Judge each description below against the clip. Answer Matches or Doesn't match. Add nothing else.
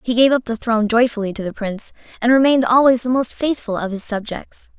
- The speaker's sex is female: Matches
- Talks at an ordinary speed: Doesn't match